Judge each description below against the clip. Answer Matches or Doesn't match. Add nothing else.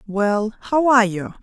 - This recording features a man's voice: Doesn't match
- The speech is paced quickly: Doesn't match